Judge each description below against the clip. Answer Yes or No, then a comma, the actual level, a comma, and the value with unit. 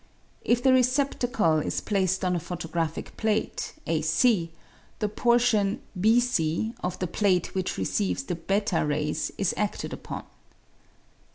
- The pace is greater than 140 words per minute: No, slow, 135 wpm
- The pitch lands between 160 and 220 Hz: Yes, high, 190 Hz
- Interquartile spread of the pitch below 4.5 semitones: No, average, 5.3 semitones